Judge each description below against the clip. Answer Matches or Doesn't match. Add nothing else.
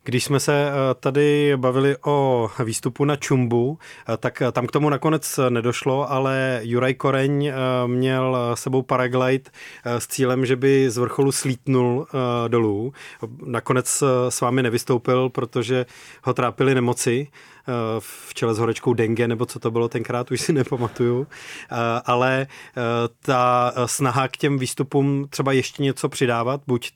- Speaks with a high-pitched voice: Doesn't match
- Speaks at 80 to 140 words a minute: Matches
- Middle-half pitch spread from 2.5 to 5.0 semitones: Doesn't match